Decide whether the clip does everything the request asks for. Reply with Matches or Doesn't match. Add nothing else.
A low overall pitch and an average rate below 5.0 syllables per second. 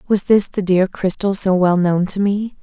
Doesn't match